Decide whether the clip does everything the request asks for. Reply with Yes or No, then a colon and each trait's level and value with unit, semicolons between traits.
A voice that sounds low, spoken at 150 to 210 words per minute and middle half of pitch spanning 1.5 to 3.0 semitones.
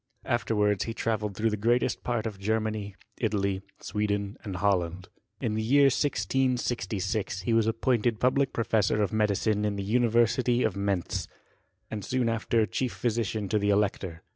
Yes: low, 110 Hz; average, 155 wpm; narrow, 2.5 semitones